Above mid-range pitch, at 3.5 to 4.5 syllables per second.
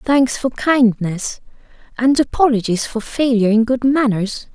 Yes: high, 240 Hz; 4.4 syllables/s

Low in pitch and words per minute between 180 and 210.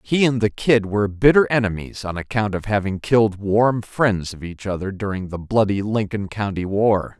Yes: low, 105 Hz; average, 190 wpm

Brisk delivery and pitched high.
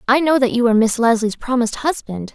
Yes: fast, 230 wpm; high, 240 Hz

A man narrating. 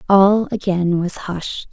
No: female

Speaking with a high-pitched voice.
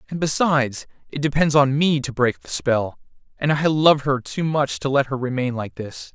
No: medium, 140 Hz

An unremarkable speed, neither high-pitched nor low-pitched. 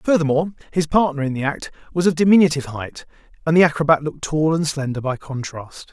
Yes: average, 195 wpm; medium, 150 Hz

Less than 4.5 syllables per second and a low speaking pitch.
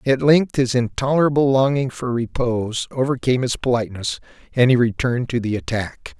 No: 5.6 syllables/s; low, 125 Hz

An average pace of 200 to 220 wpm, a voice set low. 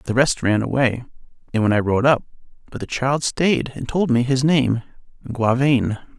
No: average, 165 wpm; low, 125 Hz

